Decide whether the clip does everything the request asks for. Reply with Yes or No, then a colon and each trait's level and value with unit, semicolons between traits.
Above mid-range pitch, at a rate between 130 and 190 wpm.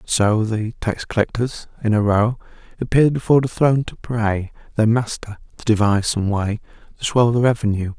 No: low, 115 Hz; average, 175 wpm